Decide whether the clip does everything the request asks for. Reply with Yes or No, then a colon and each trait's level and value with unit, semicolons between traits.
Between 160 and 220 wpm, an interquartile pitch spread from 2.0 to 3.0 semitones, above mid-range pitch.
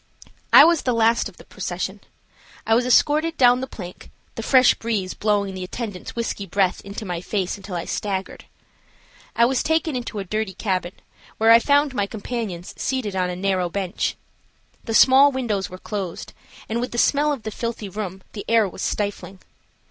No: average, 185 wpm; average, 4.2 semitones; high, 210 Hz